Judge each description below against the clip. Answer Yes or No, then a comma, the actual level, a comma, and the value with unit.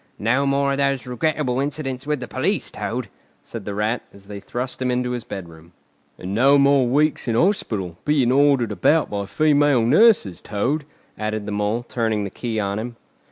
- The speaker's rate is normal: Yes, average, 185 wpm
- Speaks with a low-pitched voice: Yes, low, 125 Hz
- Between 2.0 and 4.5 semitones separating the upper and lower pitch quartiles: No, average, 5.0 semitones